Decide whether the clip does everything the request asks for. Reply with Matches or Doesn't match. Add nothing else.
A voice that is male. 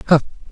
Doesn't match